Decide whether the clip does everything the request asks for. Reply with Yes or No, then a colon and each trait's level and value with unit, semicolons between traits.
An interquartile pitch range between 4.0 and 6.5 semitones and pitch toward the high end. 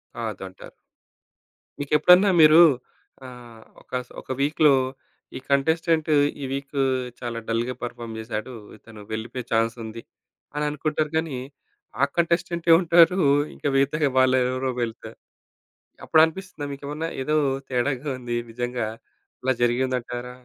No: average, 4.3 semitones; low, 130 Hz